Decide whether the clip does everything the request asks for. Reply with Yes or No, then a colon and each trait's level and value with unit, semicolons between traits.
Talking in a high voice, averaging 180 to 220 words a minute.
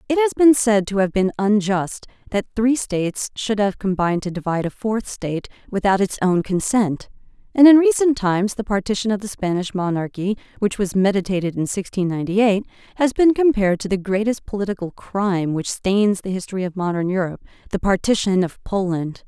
Yes: high, 200 Hz; average, 185 wpm